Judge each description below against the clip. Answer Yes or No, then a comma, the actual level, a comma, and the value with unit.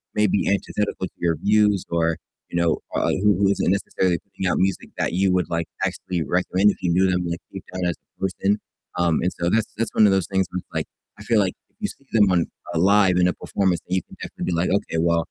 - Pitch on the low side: Yes, very low, 95 Hz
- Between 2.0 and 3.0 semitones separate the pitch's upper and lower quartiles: Yes, narrow, 2.4 semitones